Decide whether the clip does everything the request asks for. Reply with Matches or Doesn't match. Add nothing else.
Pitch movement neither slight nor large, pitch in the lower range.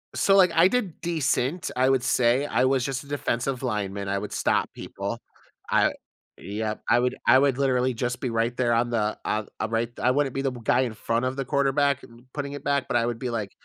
Matches